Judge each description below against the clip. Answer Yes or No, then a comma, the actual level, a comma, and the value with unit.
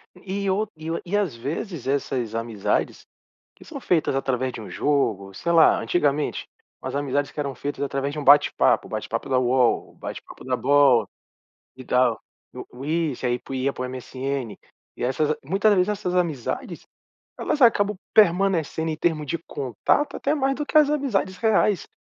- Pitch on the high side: No, medium, 145 Hz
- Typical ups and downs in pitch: No, wide, 6.1 semitones